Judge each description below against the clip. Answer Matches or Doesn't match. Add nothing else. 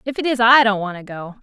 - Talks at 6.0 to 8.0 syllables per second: Matches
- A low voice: Doesn't match